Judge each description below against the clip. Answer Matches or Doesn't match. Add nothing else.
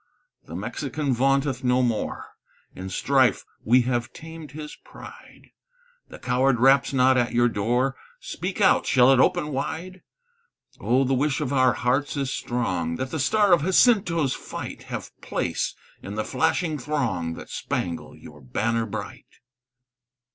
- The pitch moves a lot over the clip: Doesn't match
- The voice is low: Matches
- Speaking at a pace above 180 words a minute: Doesn't match